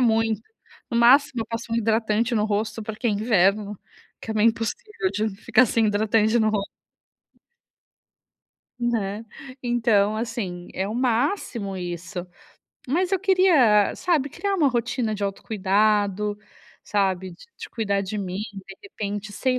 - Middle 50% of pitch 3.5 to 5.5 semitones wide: No, average, 2.9 semitones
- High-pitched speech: Yes, high, 220 Hz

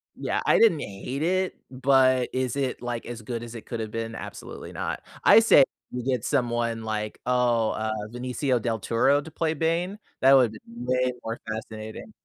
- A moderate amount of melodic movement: Yes, average, 3.1 semitones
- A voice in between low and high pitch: No, low, 125 Hz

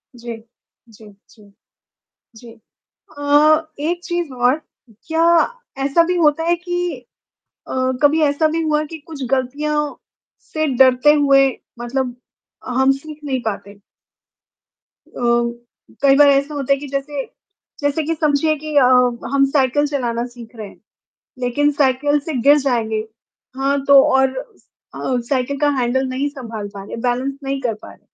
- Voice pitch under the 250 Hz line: No, very high, 275 Hz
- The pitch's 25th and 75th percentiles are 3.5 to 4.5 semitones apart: No, average, 3.0 semitones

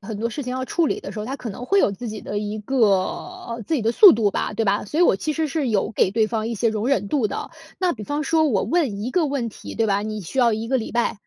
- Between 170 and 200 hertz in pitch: No, high, 230 Hz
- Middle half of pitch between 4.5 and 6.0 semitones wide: Yes, average, 4.8 semitones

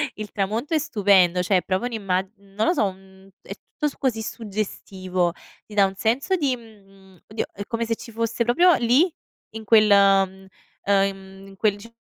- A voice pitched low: No, high, 205 Hz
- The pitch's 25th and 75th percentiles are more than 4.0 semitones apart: No, average, 3.1 semitones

